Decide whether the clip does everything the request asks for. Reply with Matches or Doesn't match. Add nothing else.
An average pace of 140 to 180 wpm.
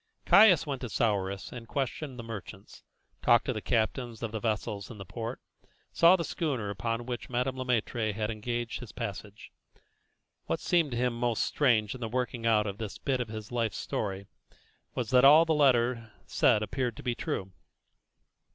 Doesn't match